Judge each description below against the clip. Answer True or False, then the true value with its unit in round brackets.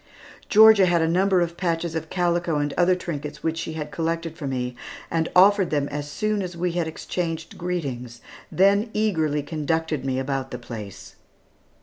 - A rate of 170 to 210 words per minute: True (175 wpm)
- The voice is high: False (165 Hz)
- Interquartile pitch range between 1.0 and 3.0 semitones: False (3.5 semitones)